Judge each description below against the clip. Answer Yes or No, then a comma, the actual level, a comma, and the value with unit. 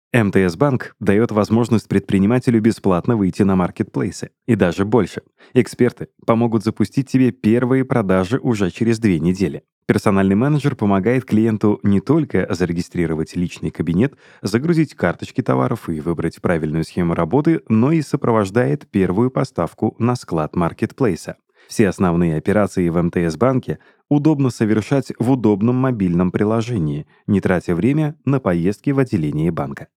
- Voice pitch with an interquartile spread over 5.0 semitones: Yes, wide, 5.5 semitones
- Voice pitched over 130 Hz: No, low, 110 Hz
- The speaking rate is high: No, average, 130 wpm